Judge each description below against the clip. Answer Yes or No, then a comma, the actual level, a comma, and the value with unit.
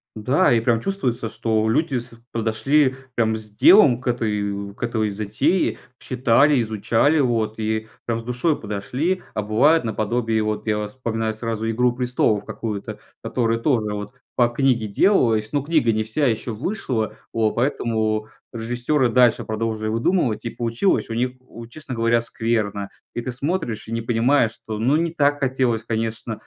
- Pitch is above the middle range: No, low, 115 Hz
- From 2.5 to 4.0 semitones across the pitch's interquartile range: Yes, average, 2.8 semitones